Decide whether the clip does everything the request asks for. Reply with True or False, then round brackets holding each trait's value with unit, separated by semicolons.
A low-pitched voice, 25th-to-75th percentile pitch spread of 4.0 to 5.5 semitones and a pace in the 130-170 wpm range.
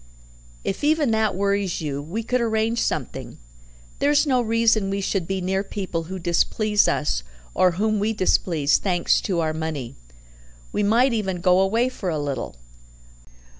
False (195 Hz; 4.4 semitones; 160 wpm)